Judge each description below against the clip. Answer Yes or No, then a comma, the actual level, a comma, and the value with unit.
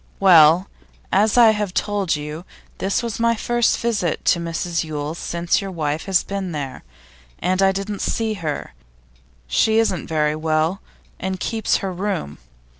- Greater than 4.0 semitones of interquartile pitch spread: Yes, average, 4.5 semitones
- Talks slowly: No, average, 155 wpm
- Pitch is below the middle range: No, medium, 185 Hz